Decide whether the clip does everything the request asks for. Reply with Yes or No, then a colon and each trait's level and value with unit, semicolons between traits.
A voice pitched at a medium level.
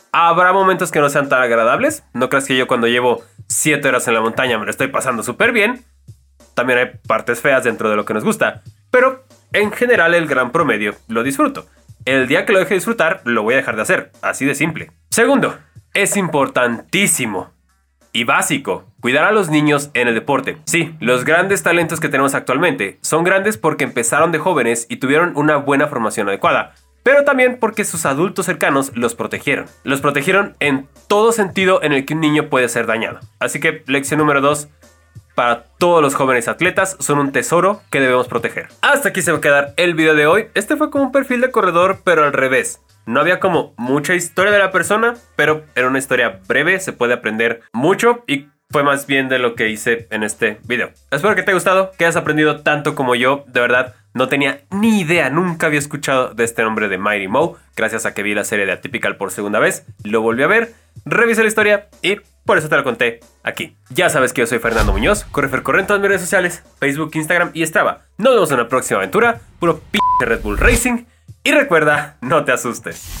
Yes: medium, 145 Hz